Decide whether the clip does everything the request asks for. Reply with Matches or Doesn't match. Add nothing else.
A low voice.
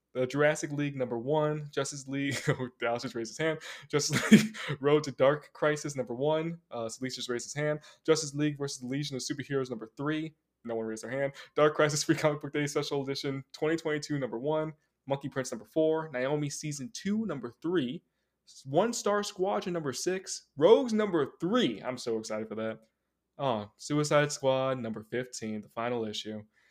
Doesn't match